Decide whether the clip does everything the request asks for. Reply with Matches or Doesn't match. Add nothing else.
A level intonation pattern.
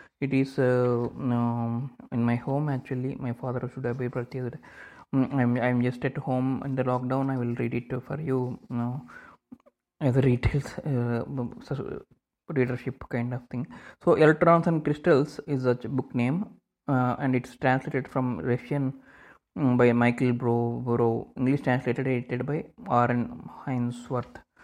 Matches